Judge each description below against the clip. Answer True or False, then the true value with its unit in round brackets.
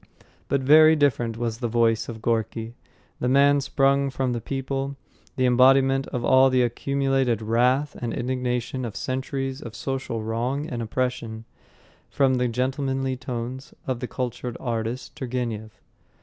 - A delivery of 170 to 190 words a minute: False (145 wpm)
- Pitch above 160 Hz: False (130 Hz)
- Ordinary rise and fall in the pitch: False (2.3 semitones)